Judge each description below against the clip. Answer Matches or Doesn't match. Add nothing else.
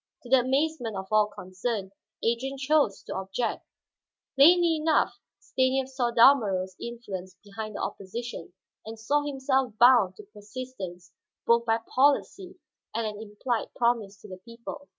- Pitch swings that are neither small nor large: Matches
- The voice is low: Doesn't match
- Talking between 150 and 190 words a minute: Doesn't match